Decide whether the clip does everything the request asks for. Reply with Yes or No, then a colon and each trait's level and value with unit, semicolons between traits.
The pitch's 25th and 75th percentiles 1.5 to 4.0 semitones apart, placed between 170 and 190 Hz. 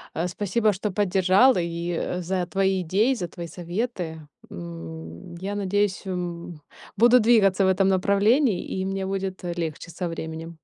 Yes: average, 2.9 semitones; medium, 185 Hz